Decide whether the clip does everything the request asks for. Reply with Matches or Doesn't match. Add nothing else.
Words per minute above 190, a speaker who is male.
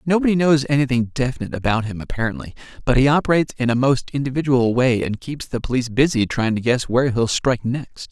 Matches